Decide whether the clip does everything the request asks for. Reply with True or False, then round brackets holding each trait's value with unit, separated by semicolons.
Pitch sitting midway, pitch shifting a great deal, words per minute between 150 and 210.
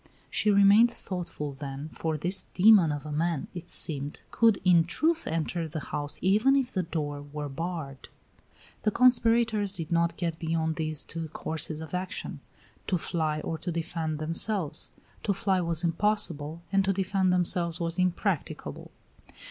False (170 Hz; 3.8 semitones; 155 wpm)